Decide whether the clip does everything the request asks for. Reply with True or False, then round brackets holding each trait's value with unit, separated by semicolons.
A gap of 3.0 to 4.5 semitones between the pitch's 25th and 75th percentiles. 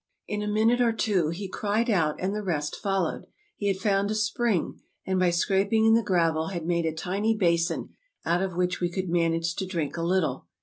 True (3.6 semitones)